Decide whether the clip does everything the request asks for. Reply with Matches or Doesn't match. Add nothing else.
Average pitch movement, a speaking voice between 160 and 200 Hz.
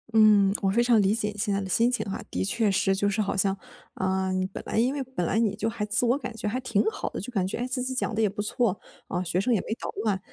Doesn't match